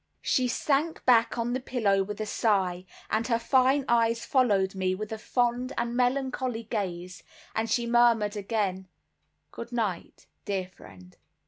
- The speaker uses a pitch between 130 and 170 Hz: No, high, 230 Hz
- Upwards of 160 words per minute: No, average, 150 wpm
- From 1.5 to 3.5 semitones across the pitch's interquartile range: No, average, 3.9 semitones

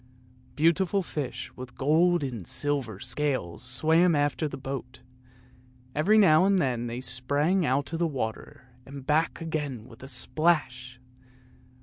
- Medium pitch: Yes, medium, 145 Hz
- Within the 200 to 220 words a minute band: No, slow, 135 wpm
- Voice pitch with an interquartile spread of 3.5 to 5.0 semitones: Yes, average, 4.3 semitones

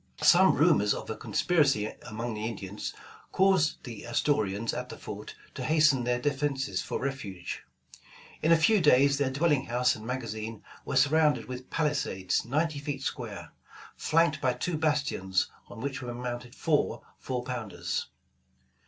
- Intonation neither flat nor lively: Yes, average, 4.7 semitones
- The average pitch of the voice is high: No, low, 130 Hz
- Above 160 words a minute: No, average, 155 wpm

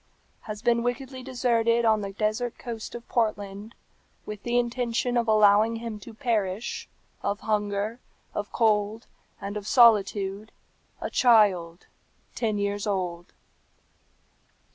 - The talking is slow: Yes, slow, 120 wpm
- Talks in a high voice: Yes, high, 215 Hz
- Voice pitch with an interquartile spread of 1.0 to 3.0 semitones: Yes, narrow, 2.6 semitones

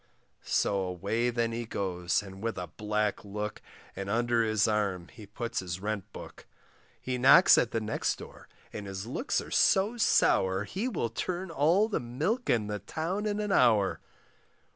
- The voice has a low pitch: Yes, low, 110 Hz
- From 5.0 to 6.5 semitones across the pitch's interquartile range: Yes, average, 5.3 semitones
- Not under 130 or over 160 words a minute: No, average, 175 wpm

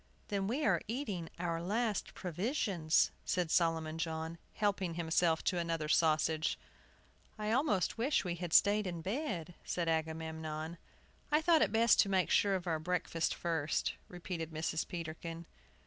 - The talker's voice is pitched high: No, medium, 170 Hz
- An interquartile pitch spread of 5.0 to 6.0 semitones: No, average, 3.8 semitones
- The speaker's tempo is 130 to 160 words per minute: Yes, average, 145 wpm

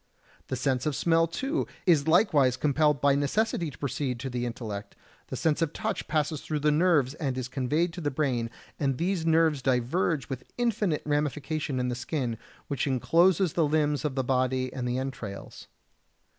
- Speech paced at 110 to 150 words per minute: No, average, 180 wpm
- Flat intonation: No, average, 4.0 semitones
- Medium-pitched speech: Yes, medium, 145 Hz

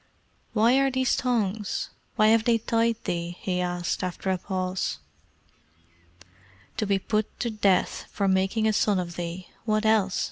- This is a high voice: Yes, high, 205 Hz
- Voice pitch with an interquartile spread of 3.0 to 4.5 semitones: Yes, average, 3.4 semitones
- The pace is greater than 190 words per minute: No, average, 165 wpm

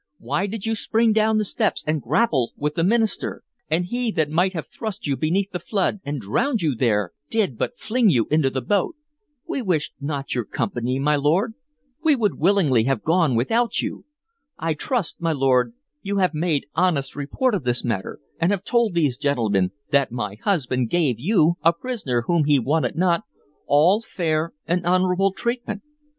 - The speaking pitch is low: No, medium, 165 Hz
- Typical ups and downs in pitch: No, wide, 6.6 semitones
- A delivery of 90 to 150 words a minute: No, average, 185 wpm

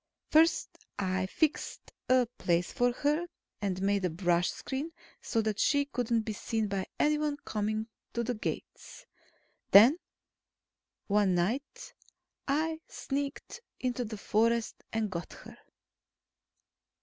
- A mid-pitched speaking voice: No, high, 225 Hz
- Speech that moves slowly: Yes, slow, 125 wpm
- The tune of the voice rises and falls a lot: Yes, wide, 5.8 semitones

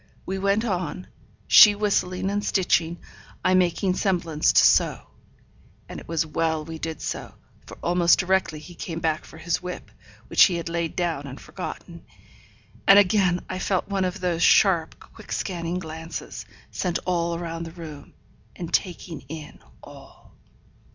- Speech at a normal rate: Yes, average, 160 wpm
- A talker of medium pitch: Yes, medium, 175 Hz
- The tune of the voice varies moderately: No, narrow, 2.2 semitones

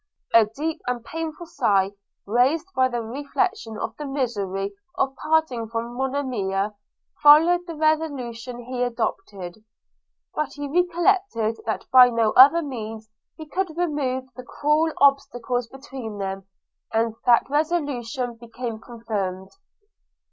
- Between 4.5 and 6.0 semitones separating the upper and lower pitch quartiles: Yes, average, 4.8 semitones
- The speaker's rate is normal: No, slow, 125 wpm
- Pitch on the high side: Yes, very high, 250 Hz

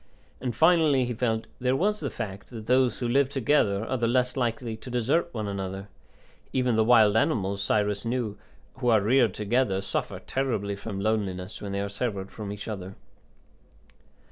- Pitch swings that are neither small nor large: Yes, average, 4.0 semitones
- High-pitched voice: No, low, 110 Hz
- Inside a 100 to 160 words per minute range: No, average, 175 wpm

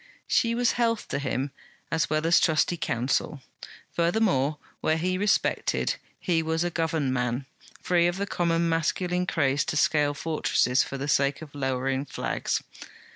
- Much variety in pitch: No, average, 4.0 semitones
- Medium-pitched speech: Yes, medium, 160 Hz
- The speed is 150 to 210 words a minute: Yes, average, 155 wpm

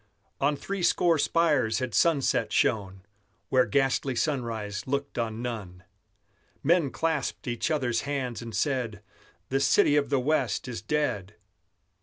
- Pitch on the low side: Yes, low, 130 Hz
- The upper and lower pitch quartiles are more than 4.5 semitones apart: No, average, 4.2 semitones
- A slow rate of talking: Yes, slow, 130 wpm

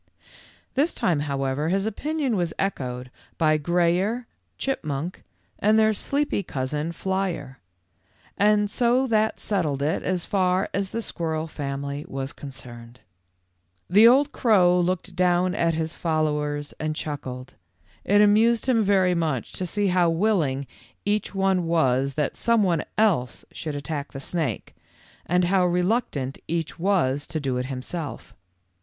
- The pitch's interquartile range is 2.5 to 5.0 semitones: No, wide, 5.6 semitones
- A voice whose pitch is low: No, medium, 170 Hz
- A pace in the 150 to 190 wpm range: No, slow, 135 wpm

